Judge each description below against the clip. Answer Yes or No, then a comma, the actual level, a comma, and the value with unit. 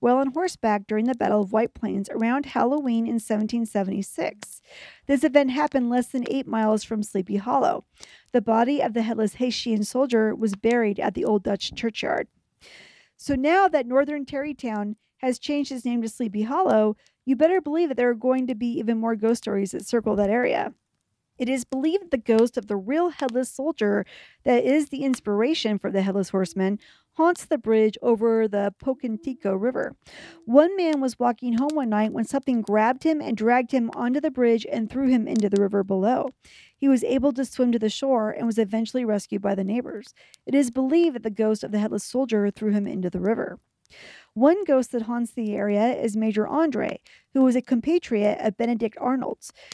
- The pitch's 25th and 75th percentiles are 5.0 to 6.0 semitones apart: No, average, 3.7 semitones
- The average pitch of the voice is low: No, high, 235 Hz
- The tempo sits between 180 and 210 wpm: Yes, average, 195 wpm